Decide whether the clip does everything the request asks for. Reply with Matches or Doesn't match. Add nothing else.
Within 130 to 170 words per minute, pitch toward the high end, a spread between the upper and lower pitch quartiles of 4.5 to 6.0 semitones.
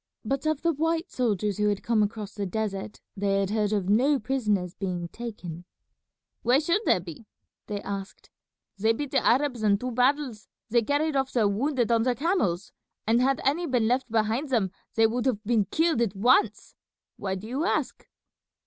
Doesn't match